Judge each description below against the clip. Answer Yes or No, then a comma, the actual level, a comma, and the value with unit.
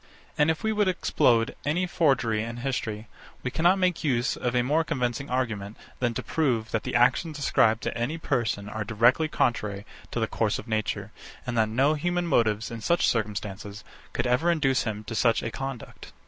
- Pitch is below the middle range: Yes, low, 120 Hz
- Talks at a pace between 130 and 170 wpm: No, average, 190 wpm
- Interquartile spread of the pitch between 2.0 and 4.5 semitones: No, average, 5.3 semitones